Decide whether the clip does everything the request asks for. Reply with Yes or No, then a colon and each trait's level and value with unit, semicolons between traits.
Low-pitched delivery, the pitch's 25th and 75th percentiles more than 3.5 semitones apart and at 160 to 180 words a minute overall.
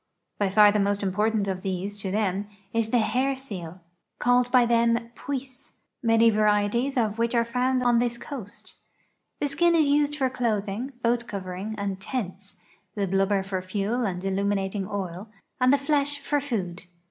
No: high, 220 Hz; average, 4.1 semitones; average, 170 wpm